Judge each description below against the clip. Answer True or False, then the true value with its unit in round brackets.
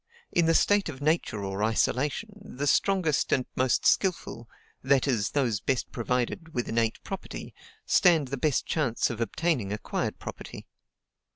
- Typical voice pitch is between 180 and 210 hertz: False (135 Hz)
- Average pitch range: False (5.8 semitones)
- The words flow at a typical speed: True (150 wpm)